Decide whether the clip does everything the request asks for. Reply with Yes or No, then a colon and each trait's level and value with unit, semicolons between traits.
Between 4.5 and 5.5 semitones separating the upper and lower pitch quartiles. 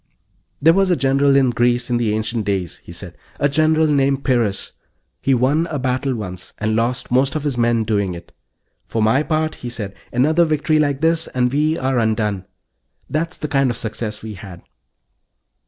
Yes: average, 4.9 semitones